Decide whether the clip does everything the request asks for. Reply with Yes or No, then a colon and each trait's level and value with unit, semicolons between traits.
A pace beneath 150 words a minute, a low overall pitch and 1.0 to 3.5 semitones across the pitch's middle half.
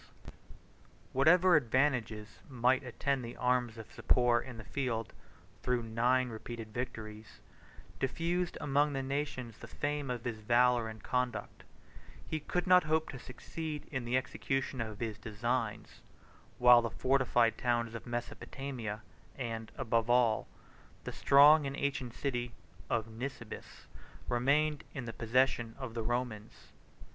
Yes: slow, 135 wpm; low, 125 Hz; average, 3.0 semitones